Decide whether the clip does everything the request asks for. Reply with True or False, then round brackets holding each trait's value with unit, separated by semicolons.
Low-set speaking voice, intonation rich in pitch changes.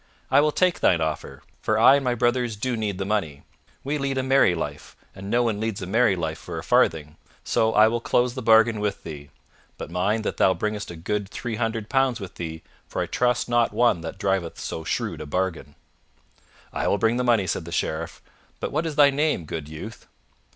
True (105 Hz; 5.9 semitones)